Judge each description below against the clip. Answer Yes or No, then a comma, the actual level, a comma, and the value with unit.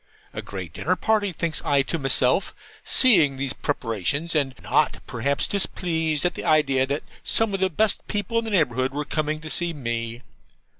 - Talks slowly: No, average, 180 wpm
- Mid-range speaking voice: Yes, medium, 150 Hz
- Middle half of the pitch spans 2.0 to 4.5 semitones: No, average, 5.3 semitones